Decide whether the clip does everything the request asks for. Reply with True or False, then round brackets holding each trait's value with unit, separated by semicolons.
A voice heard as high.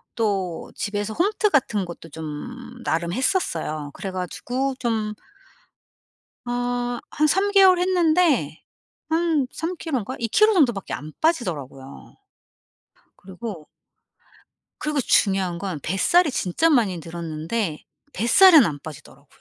True (230 Hz)